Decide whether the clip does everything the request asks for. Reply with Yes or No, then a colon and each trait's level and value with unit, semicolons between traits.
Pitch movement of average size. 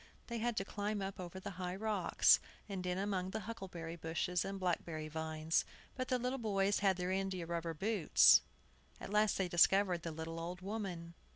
Yes: average, 3.3 semitones